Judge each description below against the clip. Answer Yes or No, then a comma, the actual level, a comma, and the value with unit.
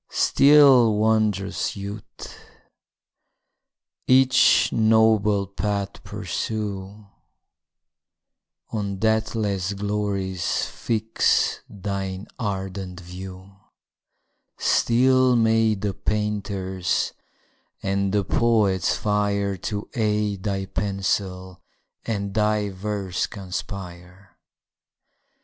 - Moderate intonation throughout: No, narrow, 2.2 semitones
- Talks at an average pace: No, slow, 70 wpm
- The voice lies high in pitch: No, low, 100 Hz